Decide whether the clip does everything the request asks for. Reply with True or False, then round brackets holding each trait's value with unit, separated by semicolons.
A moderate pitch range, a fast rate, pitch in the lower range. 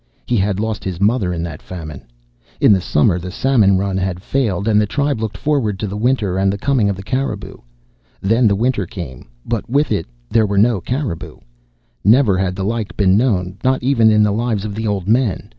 True (3.6 semitones; 215 wpm; 105 Hz)